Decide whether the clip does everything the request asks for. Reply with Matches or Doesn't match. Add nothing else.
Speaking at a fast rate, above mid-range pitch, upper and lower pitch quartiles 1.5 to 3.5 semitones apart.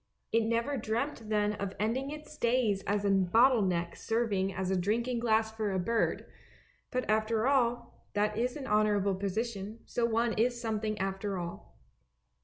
Doesn't match